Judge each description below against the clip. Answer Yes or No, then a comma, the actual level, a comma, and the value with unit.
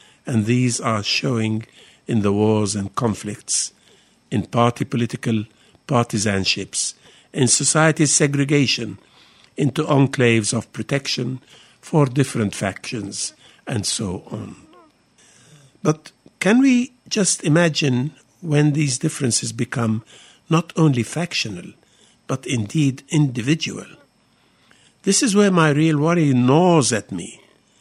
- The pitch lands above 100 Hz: Yes, low, 135 Hz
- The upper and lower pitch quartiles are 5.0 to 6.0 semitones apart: Yes, average, 5.3 semitones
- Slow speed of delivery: Yes, slow, 110 wpm